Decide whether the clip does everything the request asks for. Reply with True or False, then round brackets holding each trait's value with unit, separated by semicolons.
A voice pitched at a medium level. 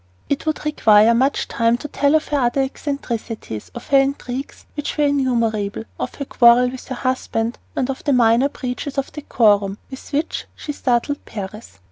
False (255 Hz)